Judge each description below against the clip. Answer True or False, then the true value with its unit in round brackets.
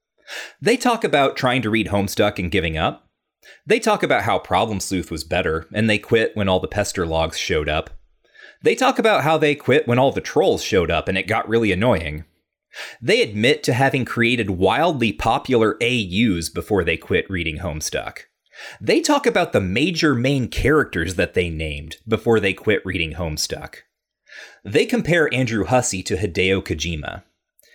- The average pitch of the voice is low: True (100 Hz)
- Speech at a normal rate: True (175 wpm)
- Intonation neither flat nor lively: False (6.8 semitones)